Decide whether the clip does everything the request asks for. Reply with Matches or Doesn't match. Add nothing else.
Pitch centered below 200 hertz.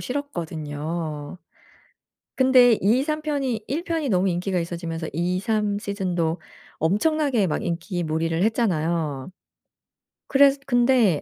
Matches